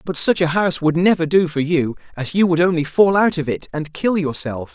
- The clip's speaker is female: No, male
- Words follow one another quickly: Yes, fast, 255 wpm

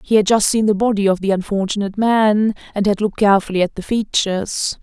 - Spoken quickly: Yes, fast, 210 wpm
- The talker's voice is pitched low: No, high, 205 Hz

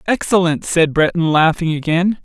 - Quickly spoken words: No, slow, 135 wpm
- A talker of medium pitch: Yes, medium, 170 Hz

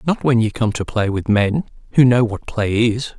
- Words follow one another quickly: Yes, fast, 245 wpm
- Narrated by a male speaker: Yes, male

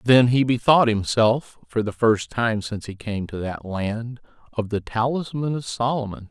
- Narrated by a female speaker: No, male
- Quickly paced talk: No, average, 180 wpm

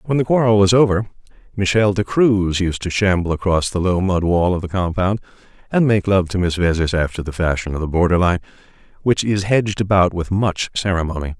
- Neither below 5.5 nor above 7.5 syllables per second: Yes, 5.8 syllables/s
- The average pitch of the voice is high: No, very low, 95 Hz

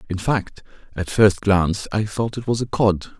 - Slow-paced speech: No, fast, 205 wpm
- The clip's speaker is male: Yes, male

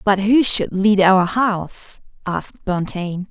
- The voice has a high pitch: Yes, high, 195 Hz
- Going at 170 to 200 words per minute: No, average, 145 wpm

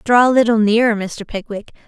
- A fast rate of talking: No, average, 190 wpm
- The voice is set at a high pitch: Yes, high, 220 Hz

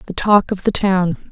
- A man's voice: No, female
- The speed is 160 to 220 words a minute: No, fast, 230 wpm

